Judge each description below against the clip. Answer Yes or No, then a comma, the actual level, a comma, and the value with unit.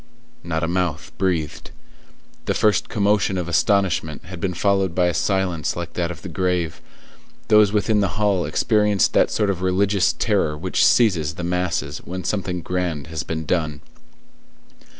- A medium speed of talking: Yes, average, 160 wpm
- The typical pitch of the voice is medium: No, very low, 90 Hz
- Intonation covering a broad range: No, average, 3.1 semitones